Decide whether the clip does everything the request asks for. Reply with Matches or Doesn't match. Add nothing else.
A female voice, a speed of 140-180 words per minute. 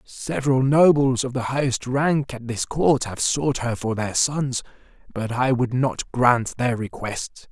Doesn't match